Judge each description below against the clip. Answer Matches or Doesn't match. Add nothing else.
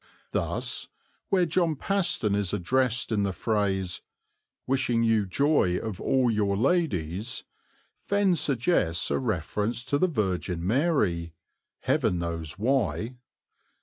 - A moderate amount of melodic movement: Doesn't match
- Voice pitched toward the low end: Matches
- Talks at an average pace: Doesn't match